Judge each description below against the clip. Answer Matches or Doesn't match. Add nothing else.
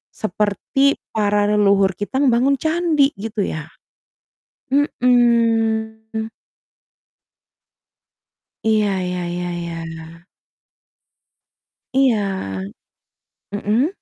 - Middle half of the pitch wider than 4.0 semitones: Matches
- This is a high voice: Matches